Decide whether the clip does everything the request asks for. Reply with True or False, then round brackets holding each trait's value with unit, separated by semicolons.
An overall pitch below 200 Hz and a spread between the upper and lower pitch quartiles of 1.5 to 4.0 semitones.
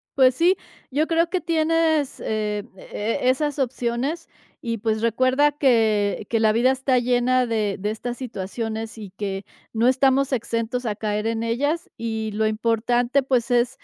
False (240 Hz; 3.4 semitones)